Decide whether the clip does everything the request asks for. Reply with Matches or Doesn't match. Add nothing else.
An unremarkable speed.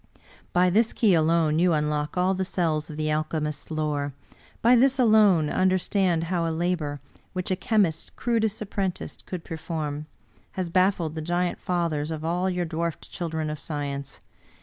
Matches